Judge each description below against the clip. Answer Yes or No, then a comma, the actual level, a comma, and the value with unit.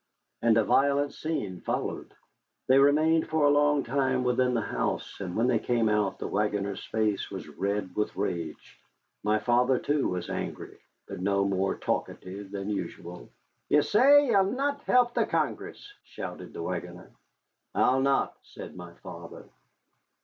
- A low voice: Yes, low, 120 Hz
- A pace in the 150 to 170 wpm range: Yes, average, 155 wpm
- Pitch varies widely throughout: Yes, wide, 6.4 semitones